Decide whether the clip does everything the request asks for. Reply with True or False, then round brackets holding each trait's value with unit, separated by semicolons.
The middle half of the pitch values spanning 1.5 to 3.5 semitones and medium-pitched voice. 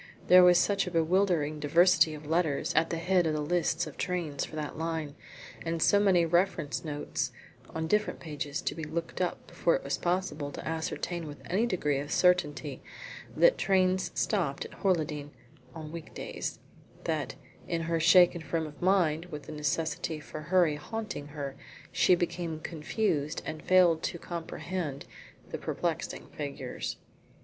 True (3.0 semitones; 165 Hz)